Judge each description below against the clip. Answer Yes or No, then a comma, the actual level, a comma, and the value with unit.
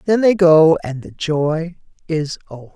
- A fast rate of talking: No, average, 175 wpm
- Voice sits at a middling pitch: Yes, medium, 160 Hz